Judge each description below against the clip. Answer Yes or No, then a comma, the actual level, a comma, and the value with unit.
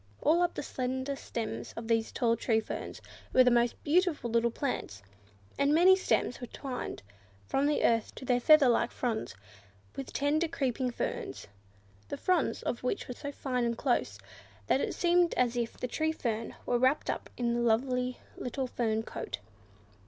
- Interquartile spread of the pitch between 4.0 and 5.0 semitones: No, average, 3.5 semitones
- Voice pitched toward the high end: Yes, very high, 250 Hz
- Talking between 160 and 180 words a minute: Yes, average, 175 wpm